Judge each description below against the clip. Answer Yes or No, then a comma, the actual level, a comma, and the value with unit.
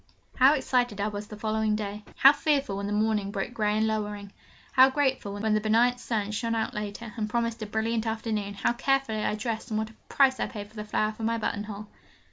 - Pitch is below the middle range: No, high, 220 Hz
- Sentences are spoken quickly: Yes, fast, 225 wpm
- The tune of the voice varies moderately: No, narrow, 2.0 semitones